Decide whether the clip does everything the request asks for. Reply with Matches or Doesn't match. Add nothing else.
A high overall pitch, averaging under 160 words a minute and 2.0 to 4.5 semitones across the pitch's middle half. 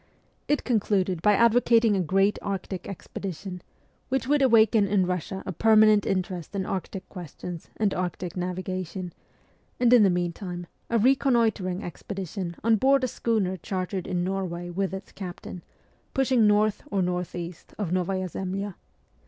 Matches